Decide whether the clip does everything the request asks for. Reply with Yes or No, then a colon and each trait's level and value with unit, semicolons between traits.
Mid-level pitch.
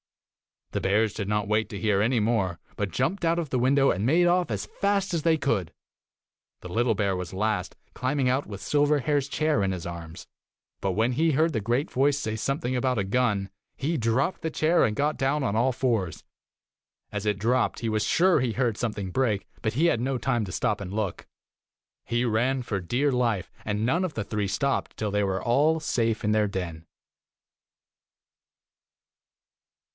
No: low, 120 Hz